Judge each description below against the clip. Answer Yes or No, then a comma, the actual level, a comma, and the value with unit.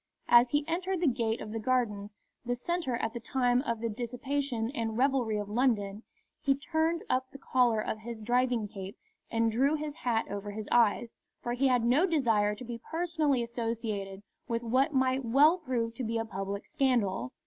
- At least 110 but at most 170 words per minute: No, average, 190 wpm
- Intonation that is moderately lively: Yes, average, 3.4 semitones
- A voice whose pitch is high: Yes, high, 240 Hz